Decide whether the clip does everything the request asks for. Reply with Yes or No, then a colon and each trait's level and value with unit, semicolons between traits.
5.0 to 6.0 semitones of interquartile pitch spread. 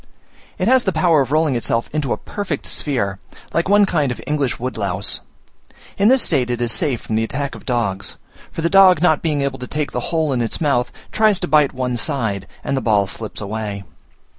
Yes: wide, 5.5 semitones